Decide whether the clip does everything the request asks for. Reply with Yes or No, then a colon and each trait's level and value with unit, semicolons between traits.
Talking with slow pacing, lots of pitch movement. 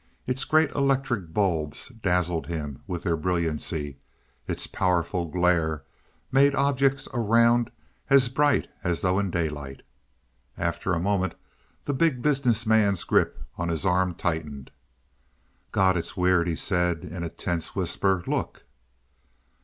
Yes: slow, 130 wpm; wide, 6.0 semitones